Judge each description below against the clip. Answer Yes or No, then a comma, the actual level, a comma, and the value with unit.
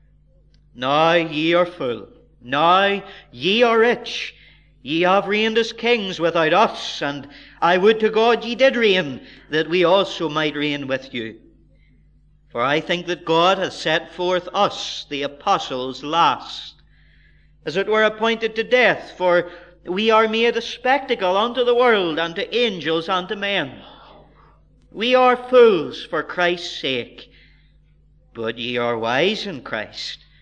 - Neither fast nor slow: Yes, average, 145 wpm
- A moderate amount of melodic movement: No, wide, 7.0 semitones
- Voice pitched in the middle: Yes, medium, 175 Hz